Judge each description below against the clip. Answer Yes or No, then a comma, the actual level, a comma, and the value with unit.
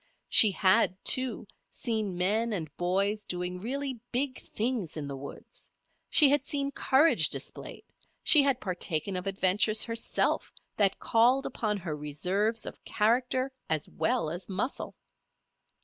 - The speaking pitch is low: No, high, 210 Hz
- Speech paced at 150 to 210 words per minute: No, slow, 135 wpm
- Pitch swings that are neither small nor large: No, wide, 5.7 semitones